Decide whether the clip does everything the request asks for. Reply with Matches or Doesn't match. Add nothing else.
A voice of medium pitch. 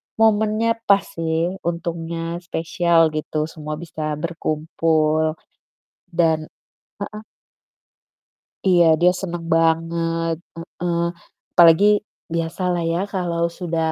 Matches